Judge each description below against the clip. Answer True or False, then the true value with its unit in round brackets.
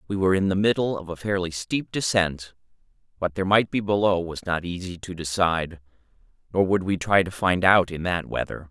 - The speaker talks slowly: False (205 wpm)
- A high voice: False (95 Hz)